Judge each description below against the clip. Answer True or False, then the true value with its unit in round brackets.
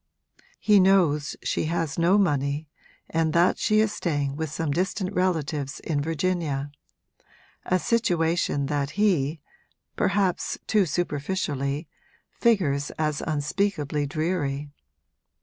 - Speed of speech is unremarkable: False (110 wpm)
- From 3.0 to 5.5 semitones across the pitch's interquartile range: True (4.2 semitones)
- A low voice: False (160 Hz)